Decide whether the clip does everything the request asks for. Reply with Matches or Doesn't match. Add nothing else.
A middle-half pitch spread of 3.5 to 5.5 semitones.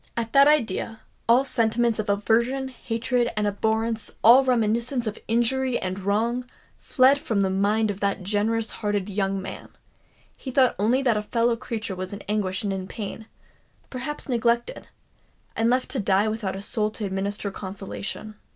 Doesn't match